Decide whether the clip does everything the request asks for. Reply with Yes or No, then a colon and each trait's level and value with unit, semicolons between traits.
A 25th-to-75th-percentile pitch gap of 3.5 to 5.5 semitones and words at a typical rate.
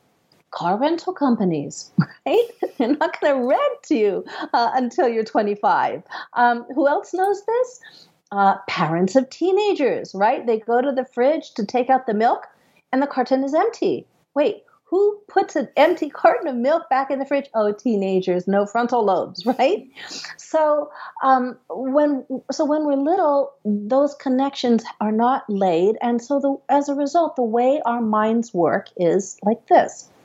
Yes: average, 4.9 semitones; average, 165 wpm